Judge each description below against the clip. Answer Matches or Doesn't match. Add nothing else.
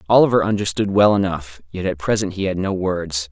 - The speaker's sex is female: Doesn't match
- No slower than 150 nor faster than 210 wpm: Matches